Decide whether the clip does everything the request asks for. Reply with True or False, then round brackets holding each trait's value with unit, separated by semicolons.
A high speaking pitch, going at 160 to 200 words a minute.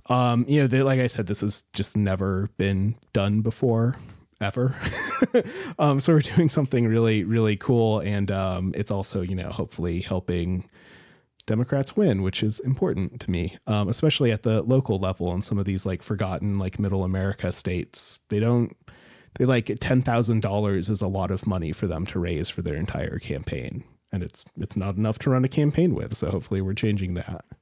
False (105 Hz; 195 wpm)